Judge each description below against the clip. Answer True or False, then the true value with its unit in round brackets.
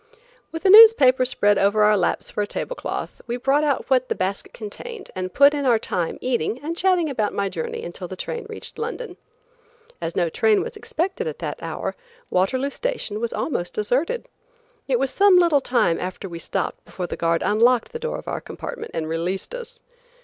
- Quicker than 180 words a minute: True (200 wpm)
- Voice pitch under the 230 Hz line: False (255 Hz)